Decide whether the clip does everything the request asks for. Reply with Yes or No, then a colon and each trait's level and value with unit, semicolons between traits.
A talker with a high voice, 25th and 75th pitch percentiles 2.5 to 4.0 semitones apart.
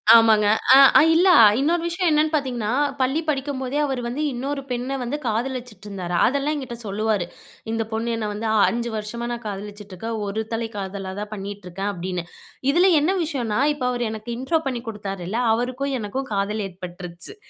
No: high, 230 Hz; average, 4.7 semitones